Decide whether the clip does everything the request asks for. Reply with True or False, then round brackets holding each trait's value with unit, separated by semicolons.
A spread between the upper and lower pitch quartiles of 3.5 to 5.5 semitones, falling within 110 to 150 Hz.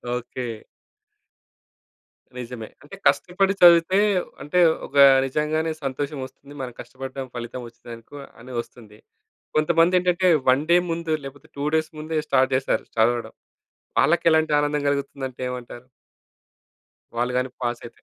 True (4.2 semitones; 140 Hz)